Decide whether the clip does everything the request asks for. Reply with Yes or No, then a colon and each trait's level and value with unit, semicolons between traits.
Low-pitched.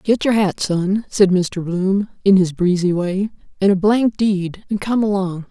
No: high, 195 Hz